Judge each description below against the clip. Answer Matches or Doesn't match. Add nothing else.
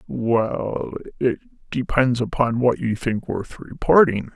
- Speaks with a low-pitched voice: Matches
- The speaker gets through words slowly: Matches